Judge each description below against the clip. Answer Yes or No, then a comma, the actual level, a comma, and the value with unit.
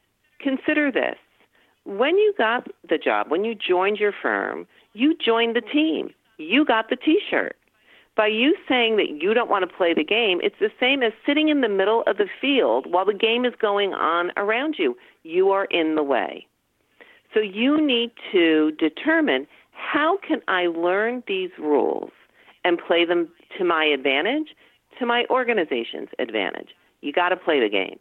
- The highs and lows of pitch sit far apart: Yes, wide, 8.2 semitones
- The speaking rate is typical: Yes, average, 175 wpm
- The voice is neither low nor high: No, very high, 250 Hz